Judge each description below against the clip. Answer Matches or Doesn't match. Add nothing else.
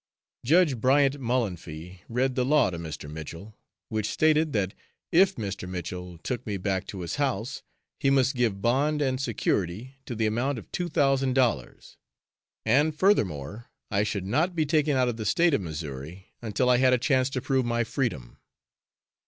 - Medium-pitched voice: Doesn't match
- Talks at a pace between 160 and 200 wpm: Matches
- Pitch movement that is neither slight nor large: Doesn't match